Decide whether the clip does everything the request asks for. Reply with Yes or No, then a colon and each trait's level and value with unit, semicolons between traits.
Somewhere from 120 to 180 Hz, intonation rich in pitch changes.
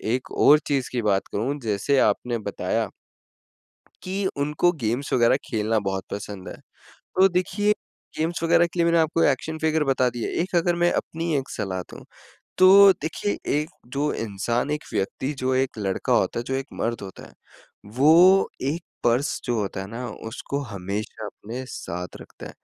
Yes: low, 135 Hz; wide, 6.6 semitones